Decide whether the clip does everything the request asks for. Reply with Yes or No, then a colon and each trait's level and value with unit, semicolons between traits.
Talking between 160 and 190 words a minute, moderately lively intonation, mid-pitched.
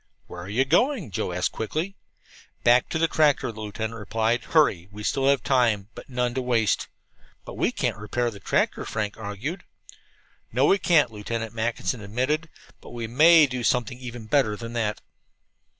No: average, 175 wpm; average, 4.0 semitones; low, 120 Hz